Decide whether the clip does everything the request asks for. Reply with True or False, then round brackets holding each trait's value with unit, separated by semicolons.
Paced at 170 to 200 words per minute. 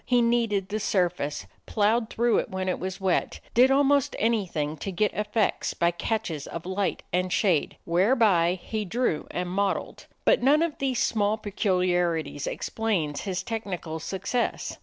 False (155 wpm)